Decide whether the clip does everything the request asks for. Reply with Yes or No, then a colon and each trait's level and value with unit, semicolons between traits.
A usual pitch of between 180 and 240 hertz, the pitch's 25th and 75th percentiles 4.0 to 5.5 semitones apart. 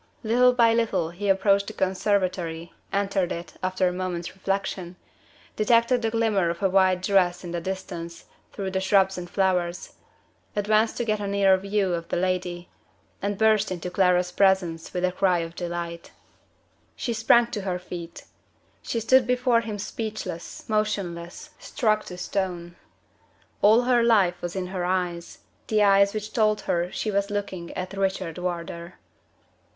No: high, 190 Hz; average, 3.1 semitones